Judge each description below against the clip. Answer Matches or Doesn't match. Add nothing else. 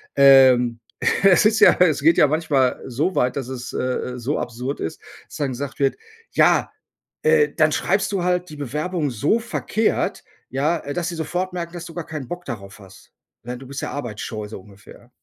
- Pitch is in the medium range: Matches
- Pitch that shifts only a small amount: Doesn't match